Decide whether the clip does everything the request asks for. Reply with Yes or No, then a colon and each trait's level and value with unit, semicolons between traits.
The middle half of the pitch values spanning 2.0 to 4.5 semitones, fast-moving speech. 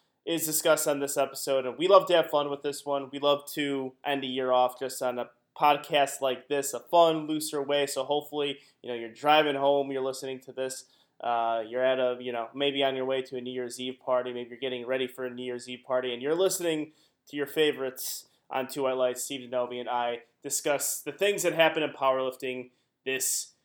Yes: narrow, 2.4 semitones; fast, 230 wpm